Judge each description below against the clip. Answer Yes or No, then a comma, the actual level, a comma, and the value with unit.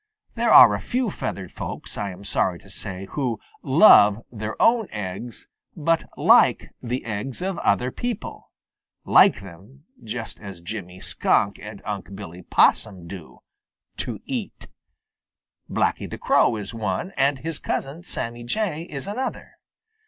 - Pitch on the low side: Yes, low, 110 Hz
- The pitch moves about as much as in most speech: No, wide, 6.7 semitones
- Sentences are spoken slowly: No, average, 145 wpm